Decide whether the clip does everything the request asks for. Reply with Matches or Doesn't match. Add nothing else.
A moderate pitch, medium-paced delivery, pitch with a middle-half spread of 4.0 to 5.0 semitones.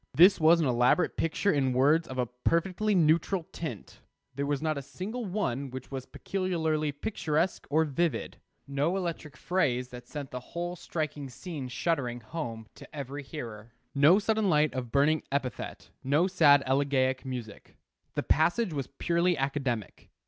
Matches